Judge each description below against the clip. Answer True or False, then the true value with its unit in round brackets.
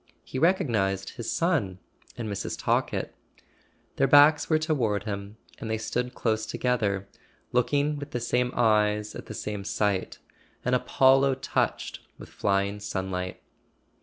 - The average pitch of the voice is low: True (110 Hz)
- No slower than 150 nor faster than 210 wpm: False (135 wpm)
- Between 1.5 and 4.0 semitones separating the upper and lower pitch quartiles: False (4.8 semitones)